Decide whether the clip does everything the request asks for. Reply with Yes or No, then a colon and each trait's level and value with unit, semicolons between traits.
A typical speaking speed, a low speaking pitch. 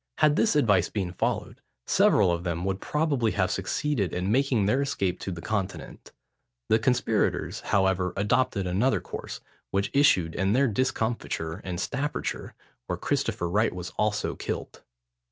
Yes: average, 150 wpm; low, 100 Hz